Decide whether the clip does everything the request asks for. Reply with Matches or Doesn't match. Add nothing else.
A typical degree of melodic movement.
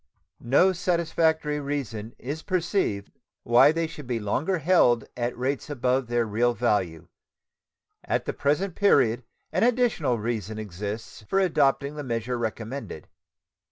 Doesn't match